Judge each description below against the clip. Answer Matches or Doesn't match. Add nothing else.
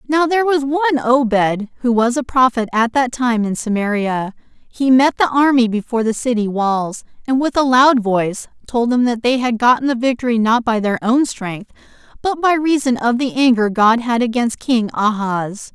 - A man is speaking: Doesn't match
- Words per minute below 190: Doesn't match